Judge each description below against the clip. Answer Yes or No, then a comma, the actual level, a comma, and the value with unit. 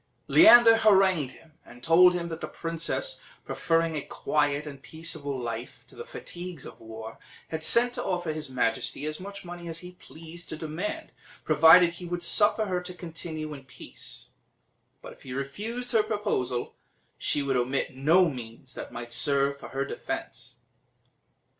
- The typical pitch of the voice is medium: Yes, medium, 165 Hz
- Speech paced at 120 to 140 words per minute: No, average, 165 wpm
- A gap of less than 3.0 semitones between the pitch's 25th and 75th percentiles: No, average, 4.7 semitones